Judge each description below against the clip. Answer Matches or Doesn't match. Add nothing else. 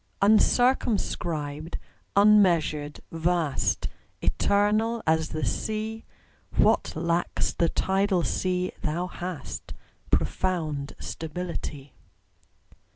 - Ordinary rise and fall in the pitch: Matches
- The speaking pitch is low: Doesn't match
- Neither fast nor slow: Doesn't match